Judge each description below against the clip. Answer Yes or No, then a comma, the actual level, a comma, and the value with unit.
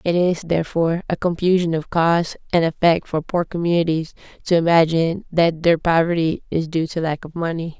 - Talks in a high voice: No, medium, 165 Hz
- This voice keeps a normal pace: Yes, average, 175 wpm